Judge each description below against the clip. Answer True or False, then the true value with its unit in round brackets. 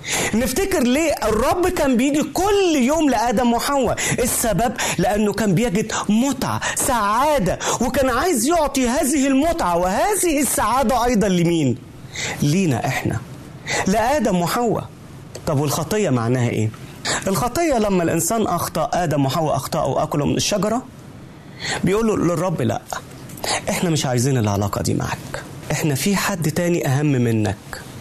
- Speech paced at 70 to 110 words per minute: False (120 wpm)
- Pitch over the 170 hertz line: True (190 Hz)